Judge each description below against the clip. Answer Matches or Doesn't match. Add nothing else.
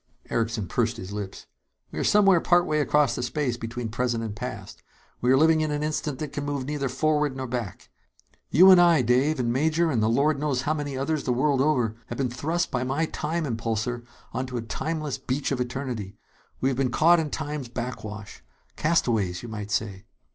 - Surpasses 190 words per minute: Matches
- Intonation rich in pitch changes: Doesn't match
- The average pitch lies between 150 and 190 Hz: Doesn't match